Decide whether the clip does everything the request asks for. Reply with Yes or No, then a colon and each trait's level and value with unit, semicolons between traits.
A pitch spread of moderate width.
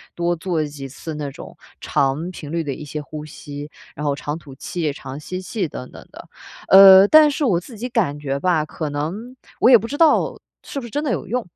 No: wide, 6.0 semitones